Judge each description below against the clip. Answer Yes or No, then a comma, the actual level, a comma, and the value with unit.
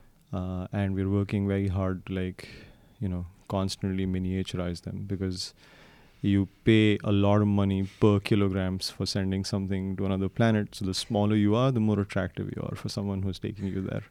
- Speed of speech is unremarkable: Yes, average, 185 wpm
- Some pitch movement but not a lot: No, narrow, 1.5 semitones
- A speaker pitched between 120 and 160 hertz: No, low, 100 Hz